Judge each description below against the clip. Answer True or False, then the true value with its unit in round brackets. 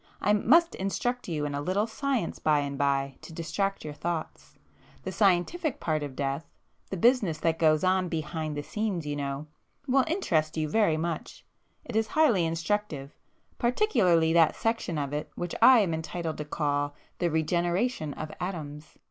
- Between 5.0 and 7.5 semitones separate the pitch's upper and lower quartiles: True (5.5 semitones)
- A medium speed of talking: True (160 wpm)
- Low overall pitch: False (165 Hz)